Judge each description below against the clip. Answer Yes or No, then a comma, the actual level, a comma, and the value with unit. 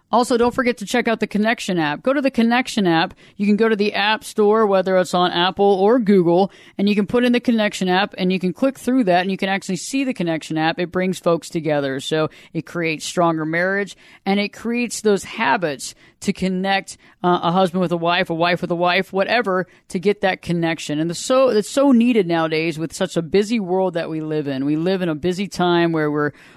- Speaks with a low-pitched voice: No, high, 190 Hz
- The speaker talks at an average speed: No, fast, 245 wpm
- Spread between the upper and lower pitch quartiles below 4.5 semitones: Yes, average, 3.9 semitones